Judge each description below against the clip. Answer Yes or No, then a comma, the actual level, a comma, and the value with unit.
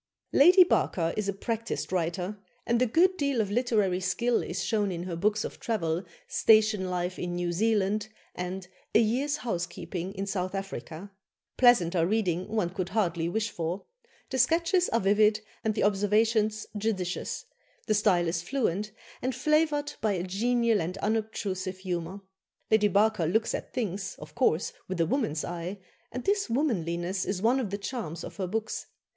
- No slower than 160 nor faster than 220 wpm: Yes, average, 170 wpm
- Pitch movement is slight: No, average, 4.0 semitones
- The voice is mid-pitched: No, high, 205 Hz